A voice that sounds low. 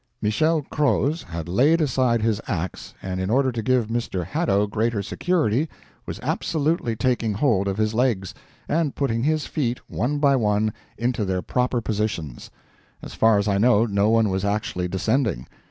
Yes: low, 115 Hz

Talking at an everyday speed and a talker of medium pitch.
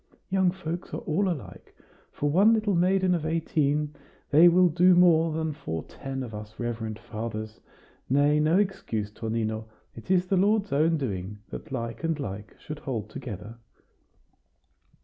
Yes: average, 155 wpm; medium, 150 Hz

